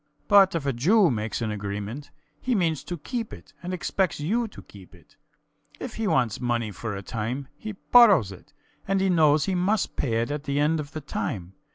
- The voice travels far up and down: Yes, wide, 8.8 semitones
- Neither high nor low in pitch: Yes, medium, 145 Hz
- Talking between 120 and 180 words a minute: No, fast, 205 wpm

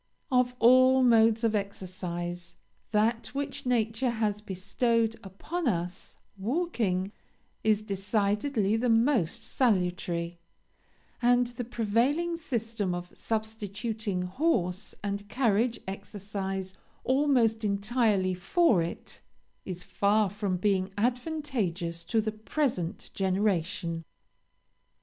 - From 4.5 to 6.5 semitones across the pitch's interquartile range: No, average, 4.1 semitones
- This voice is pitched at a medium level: No, high, 215 Hz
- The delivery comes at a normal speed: No, slow, 100 wpm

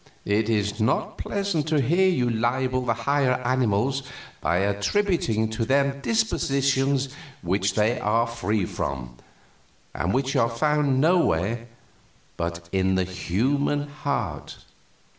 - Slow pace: Yes, slow, 120 wpm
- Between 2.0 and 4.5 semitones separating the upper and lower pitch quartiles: No, average, 5.3 semitones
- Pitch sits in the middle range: No, low, 120 Hz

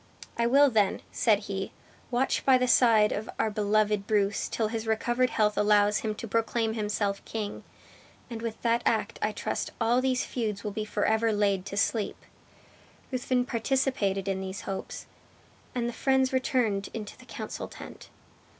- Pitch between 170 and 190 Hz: No, high, 220 Hz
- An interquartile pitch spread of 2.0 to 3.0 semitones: Yes, narrow, 2.6 semitones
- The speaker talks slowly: No, average, 165 wpm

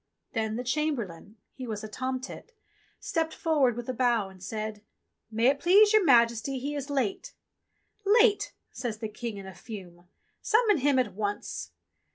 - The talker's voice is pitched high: Yes, high, 245 Hz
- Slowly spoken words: No, average, 185 wpm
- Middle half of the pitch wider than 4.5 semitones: Yes, average, 5.2 semitones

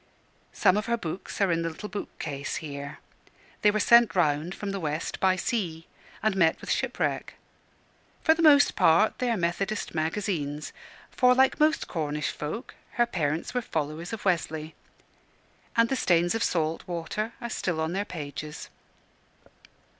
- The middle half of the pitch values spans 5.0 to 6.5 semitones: Yes, wide, 5.5 semitones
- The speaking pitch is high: No, medium, 175 Hz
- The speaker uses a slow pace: No, average, 160 wpm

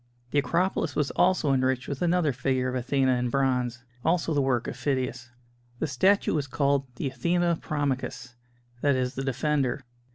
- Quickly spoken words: No, average, 165 wpm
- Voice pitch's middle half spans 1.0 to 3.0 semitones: Yes, average, 2.7 semitones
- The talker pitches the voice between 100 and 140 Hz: Yes, low, 135 Hz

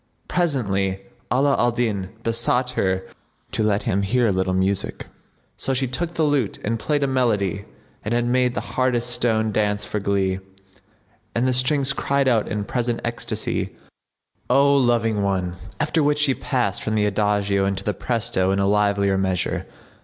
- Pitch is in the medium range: No, low, 115 Hz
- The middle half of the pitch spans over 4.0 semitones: Yes, average, 4.4 semitones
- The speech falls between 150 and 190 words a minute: Yes, average, 170 wpm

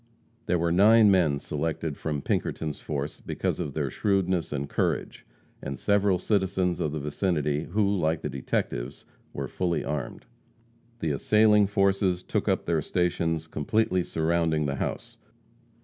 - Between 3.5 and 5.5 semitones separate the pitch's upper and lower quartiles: Yes, average, 4.2 semitones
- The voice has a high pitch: No, very low, 85 Hz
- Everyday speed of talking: Yes, average, 145 wpm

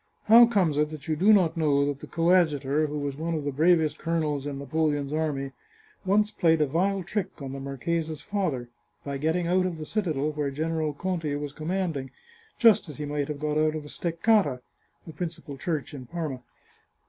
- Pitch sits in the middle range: Yes, medium, 155 Hz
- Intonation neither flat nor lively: Yes, average, 3.2 semitones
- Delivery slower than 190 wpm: No, average, 195 wpm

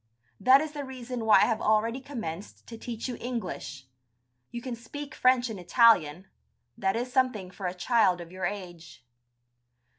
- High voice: Yes, high, 230 Hz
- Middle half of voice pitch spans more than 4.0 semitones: Yes, average, 5.2 semitones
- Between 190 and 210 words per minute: No, average, 170 wpm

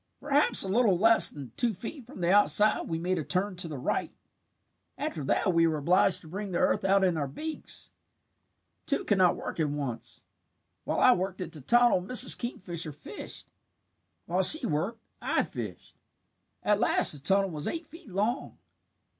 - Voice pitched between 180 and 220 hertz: Yes, medium, 185 Hz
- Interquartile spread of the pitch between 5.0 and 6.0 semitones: Yes, average, 5.3 semitones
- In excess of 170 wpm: Yes, average, 180 wpm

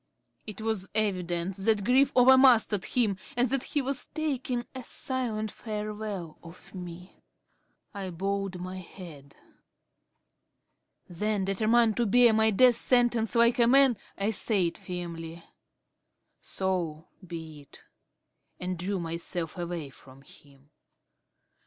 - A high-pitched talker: Yes, high, 200 Hz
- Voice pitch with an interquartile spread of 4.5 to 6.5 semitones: Yes, average, 5.1 semitones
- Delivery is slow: Yes, slow, 120 wpm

